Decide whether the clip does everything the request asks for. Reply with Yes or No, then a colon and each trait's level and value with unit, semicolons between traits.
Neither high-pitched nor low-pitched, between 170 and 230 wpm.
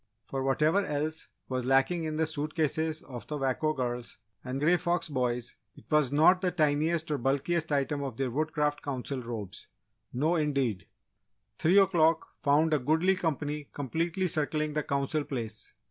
No: medium, 150 Hz; average, 160 wpm